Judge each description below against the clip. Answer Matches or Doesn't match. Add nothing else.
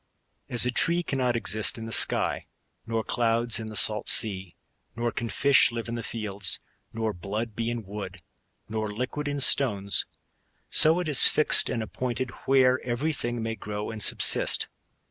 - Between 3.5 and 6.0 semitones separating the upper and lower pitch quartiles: Doesn't match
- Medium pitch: Doesn't match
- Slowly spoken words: Doesn't match